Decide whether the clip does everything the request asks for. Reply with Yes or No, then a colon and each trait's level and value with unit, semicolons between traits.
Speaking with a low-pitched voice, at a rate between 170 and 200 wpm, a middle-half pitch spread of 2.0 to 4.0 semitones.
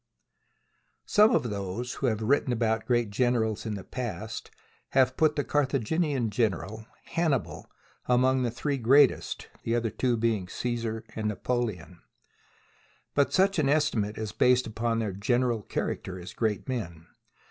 No: low, 120 Hz; average, 145 wpm; average, 3.3 semitones